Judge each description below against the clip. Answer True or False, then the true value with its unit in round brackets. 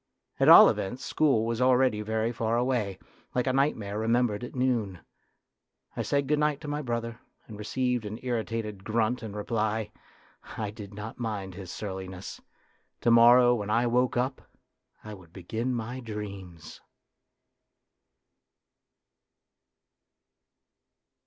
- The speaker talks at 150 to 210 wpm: False (135 wpm)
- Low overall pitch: True (115 Hz)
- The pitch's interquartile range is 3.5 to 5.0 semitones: False (3.0 semitones)